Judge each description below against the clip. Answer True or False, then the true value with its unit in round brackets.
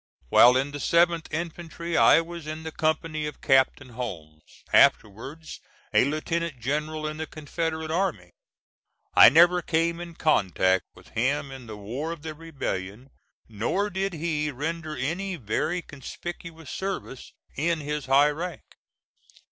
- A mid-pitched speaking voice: True (155 Hz)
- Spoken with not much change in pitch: False (4.0 semitones)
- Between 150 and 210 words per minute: False (140 wpm)